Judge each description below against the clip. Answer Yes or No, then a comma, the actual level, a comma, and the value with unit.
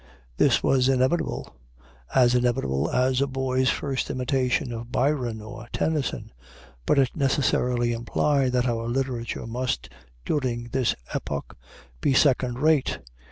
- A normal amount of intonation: No, narrow, 2.1 semitones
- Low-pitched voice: Yes, low, 125 Hz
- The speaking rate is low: Yes, slow, 125 wpm